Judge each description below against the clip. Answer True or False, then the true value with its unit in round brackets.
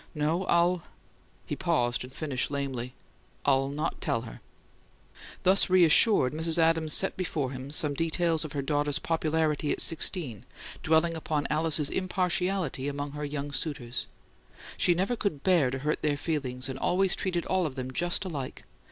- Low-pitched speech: False (155 Hz)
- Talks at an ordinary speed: True (160 wpm)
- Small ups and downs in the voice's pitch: False (3.6 semitones)